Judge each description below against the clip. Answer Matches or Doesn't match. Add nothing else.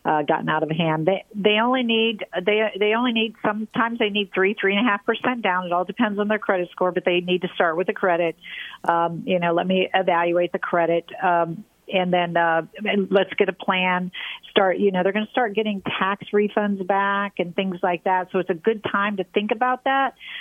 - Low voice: Doesn't match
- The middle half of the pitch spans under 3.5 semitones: Matches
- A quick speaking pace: Matches